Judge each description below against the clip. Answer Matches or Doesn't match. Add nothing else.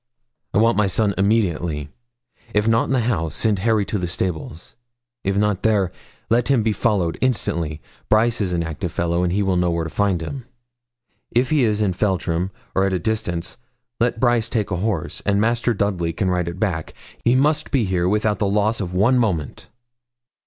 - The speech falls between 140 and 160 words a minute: Doesn't match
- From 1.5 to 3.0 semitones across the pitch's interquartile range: Doesn't match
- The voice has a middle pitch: Doesn't match